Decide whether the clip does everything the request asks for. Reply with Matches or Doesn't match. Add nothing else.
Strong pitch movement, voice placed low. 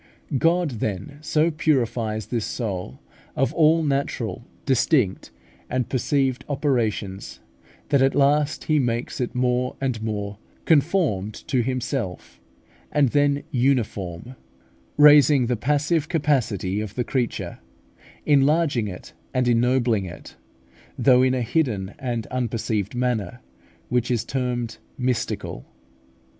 Doesn't match